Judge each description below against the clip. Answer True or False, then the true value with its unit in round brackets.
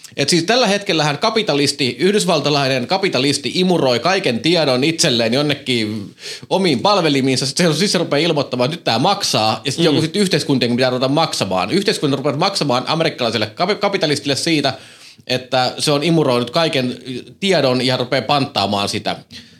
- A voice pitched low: False (145 Hz)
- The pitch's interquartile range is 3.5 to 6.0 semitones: True (4.7 semitones)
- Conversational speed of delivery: True (140 wpm)